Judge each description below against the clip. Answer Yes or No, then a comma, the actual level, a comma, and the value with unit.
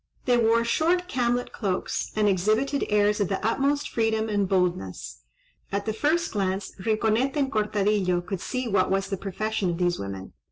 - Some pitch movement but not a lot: Yes, average, 3.6 semitones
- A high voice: Yes, high, 215 Hz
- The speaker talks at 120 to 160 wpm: No, average, 170 wpm